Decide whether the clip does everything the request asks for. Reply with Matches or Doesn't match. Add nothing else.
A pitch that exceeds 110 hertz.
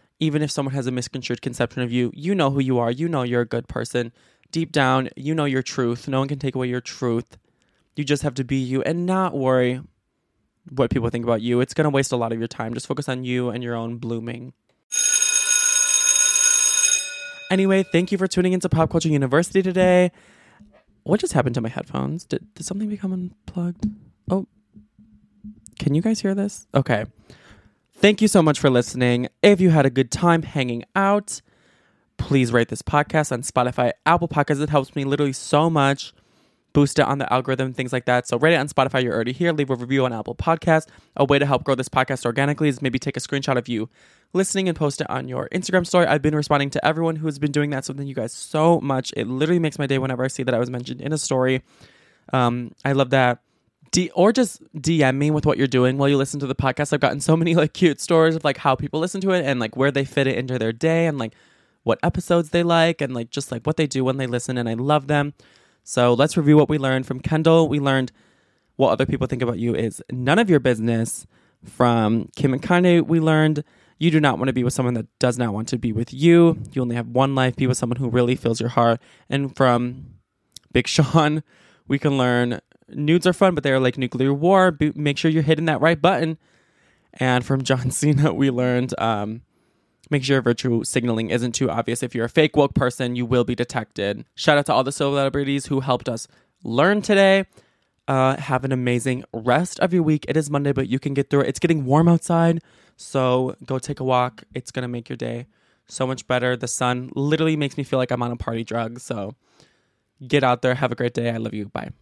Matches